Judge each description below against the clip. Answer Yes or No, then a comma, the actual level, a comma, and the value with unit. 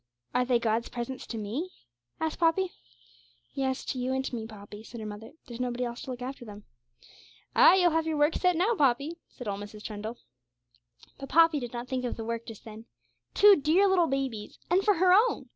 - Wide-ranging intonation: Yes, wide, 6.1 semitones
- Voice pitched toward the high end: Yes, very high, 255 Hz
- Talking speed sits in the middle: No, fast, 210 wpm